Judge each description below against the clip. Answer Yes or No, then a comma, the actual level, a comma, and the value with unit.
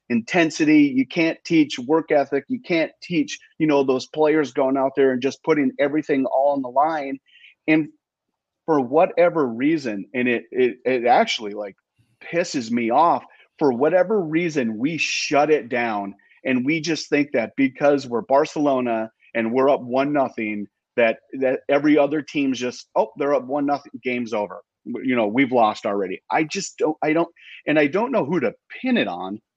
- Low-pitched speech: No, medium, 145 Hz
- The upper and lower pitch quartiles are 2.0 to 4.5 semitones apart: Yes, average, 4.2 semitones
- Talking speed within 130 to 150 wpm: No, average, 180 wpm